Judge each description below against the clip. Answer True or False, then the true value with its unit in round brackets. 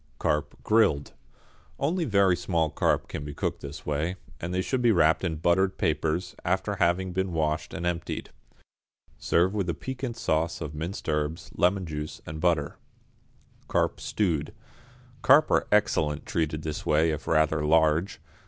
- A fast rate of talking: False (155 wpm)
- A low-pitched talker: True (85 Hz)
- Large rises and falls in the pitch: False (3.5 semitones)